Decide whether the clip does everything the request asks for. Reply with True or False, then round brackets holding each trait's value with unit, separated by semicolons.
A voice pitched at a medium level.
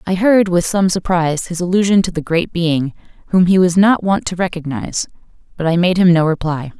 True (175 Hz)